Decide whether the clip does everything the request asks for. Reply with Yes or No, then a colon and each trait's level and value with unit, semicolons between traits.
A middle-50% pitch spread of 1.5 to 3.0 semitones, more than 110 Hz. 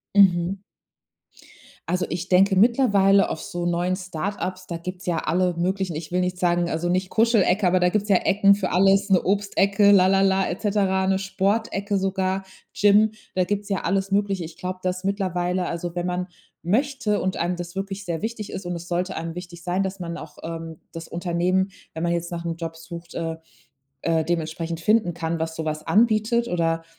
Yes: narrow, 2.4 semitones; medium, 185 Hz